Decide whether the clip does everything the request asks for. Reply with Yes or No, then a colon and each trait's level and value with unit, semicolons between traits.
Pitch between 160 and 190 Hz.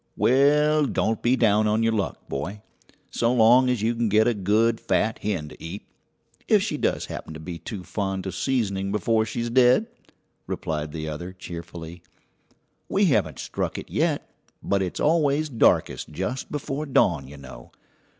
No: low, 110 Hz